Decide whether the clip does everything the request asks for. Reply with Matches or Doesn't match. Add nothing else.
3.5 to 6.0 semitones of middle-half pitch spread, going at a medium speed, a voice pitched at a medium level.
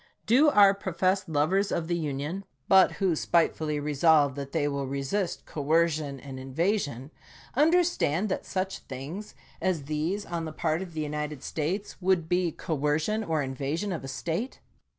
Matches